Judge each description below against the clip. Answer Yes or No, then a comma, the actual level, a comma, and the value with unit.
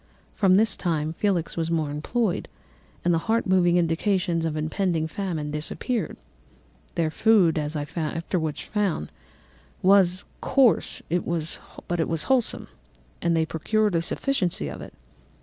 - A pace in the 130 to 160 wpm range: Yes, slow, 135 wpm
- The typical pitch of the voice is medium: Yes, medium, 170 Hz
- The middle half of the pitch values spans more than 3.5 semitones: Yes, average, 3.9 semitones